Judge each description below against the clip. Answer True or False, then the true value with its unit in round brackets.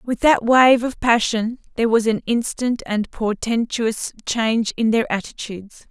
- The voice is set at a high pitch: True (230 Hz)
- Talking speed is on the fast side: False (155 wpm)